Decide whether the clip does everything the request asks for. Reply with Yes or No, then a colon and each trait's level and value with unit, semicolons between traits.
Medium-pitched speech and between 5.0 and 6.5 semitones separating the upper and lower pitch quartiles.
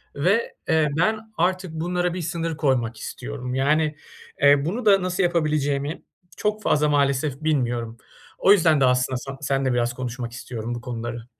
Yes: medium, 145 Hz; average, 5.3 semitones